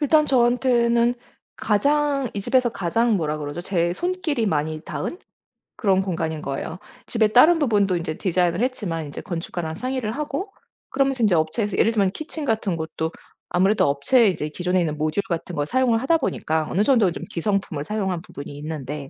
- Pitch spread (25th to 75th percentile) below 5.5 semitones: No, wide, 7.2 semitones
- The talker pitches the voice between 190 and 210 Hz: Yes, high, 195 Hz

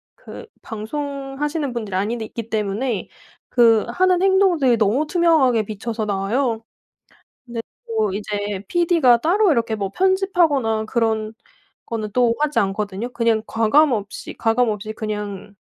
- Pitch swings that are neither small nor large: Yes, average, 5.0 semitones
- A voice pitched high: Yes, high, 230 Hz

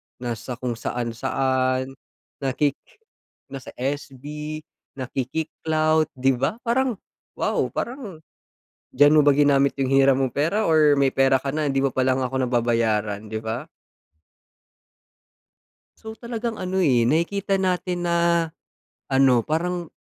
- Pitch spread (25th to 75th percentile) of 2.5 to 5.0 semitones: Yes, average, 4.2 semitones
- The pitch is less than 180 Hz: Yes, medium, 140 Hz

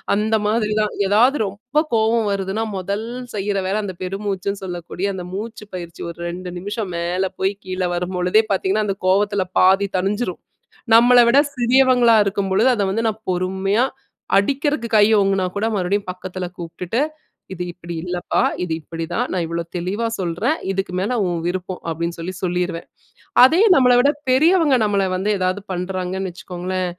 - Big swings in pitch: No, average, 3.3 semitones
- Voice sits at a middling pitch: No, high, 195 Hz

